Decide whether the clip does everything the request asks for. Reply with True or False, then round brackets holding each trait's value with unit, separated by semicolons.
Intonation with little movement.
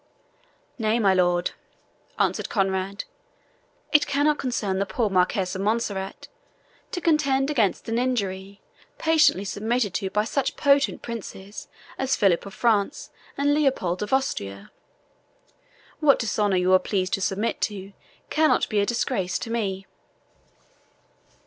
False (5.4 semitones)